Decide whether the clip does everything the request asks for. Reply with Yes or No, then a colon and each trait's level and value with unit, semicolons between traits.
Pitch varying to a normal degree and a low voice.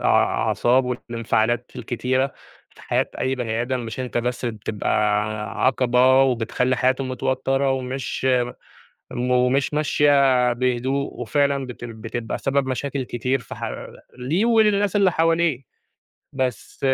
No: narrow, 2.1 semitones; low, 130 Hz